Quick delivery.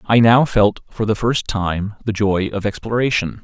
No: average, 190 wpm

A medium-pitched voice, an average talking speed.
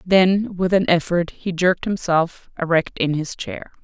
Yes: medium, 180 Hz; average, 170 wpm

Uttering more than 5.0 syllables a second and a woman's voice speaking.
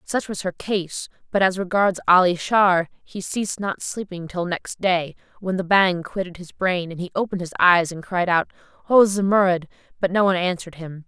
Yes: 5.2 syllables/s; female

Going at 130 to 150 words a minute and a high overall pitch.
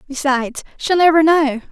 Yes: average, 140 wpm; very high, 290 Hz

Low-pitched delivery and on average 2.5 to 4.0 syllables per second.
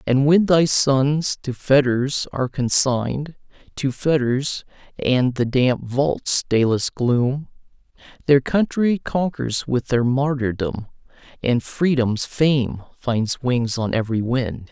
Yes: low, 130 Hz; 3.5 syllables/s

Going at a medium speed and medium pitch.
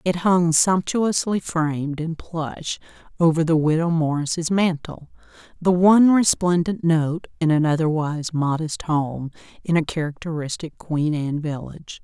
No: slow, 130 wpm; medium, 160 Hz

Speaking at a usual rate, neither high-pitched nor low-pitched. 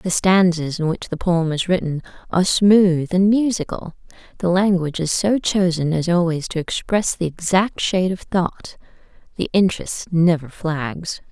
Yes: average, 160 wpm; medium, 175 Hz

